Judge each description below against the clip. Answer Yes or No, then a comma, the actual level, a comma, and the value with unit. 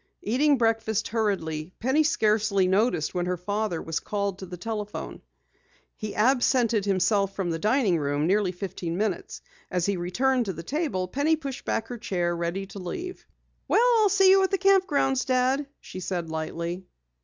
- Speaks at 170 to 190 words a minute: Yes, average, 175 wpm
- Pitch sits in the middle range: No, high, 205 Hz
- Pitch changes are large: Yes, wide, 6.2 semitones